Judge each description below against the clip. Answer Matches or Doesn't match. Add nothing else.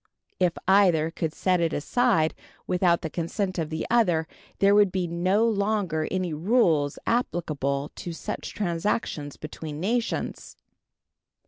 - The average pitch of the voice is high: Doesn't match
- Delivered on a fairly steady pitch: Doesn't match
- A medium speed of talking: Doesn't match